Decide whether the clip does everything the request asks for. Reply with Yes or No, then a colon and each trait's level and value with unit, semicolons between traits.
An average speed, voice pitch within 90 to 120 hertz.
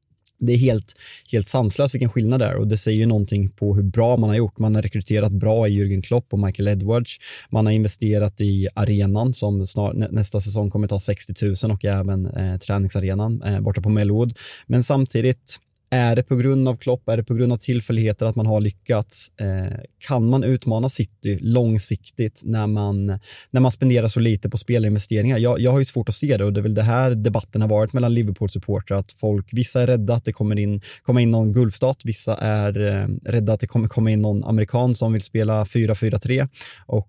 No: fast, 210 wpm; low, 110 Hz